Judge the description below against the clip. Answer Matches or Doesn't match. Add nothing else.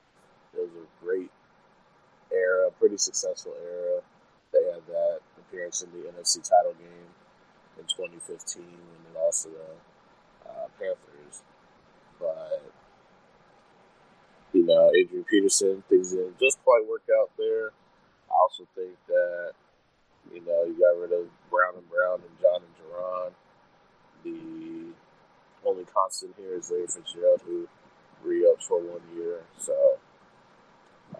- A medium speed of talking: Doesn't match